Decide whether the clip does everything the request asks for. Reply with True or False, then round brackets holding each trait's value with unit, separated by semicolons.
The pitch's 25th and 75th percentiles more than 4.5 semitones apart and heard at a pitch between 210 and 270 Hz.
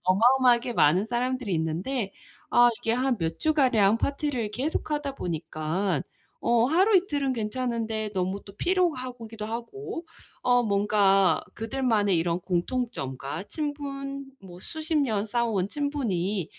True (5.6 semitones; 230 Hz)